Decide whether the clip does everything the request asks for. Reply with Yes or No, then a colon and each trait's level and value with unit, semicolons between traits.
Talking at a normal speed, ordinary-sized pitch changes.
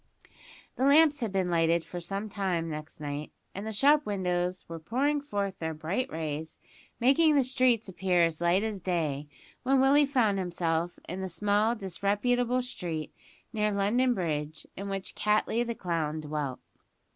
No: average, 160 wpm; wide, 6.2 semitones